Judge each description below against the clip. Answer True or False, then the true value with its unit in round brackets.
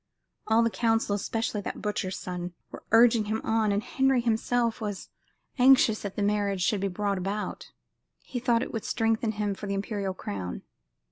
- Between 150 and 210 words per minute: True (180 wpm)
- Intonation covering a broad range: False (2.5 semitones)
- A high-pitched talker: True (210 Hz)